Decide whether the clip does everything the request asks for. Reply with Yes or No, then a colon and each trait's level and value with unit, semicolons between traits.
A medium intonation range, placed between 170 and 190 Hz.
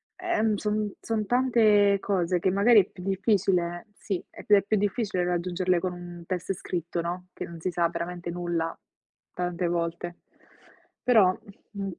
Yes: average, 3.0 semitones; medium, 185 Hz